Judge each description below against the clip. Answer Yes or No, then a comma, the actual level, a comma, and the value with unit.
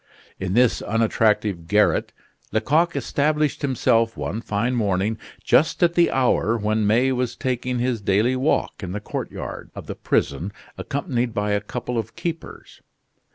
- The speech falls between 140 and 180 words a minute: Yes, average, 150 wpm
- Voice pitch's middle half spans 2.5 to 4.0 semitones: Yes, average, 3.6 semitones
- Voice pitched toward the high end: No, low, 115 Hz